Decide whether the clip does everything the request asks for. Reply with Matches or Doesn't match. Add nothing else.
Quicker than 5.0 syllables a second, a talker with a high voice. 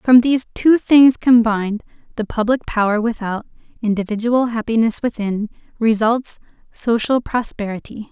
Doesn't match